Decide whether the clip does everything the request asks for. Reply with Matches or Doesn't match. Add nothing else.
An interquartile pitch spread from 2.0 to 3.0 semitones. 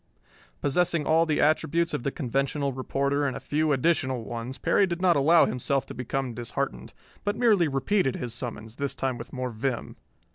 Doesn't match